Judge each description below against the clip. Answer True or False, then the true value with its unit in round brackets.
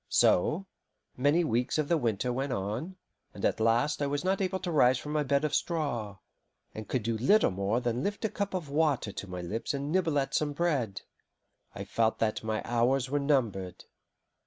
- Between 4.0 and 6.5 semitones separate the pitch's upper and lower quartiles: True (5.3 semitones)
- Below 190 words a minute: False (200 wpm)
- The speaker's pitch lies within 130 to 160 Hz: True (135 Hz)